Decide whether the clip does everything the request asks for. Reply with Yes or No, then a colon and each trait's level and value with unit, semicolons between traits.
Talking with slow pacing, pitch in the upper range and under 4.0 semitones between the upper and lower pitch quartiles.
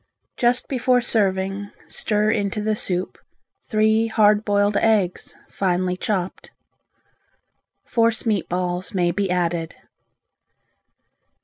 Yes: slow, 100 wpm; high, 205 Hz; average, 3.0 semitones